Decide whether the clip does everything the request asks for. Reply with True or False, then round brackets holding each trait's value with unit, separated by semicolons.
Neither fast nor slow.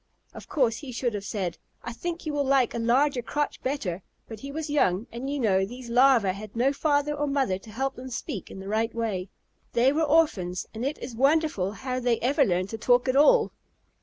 False (220 wpm)